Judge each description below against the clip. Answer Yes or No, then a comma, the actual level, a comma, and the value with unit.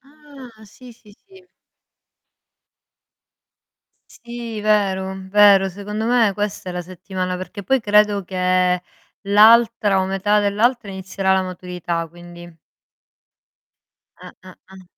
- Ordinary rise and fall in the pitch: Yes, average, 3.0 semitones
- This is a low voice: No, high, 200 Hz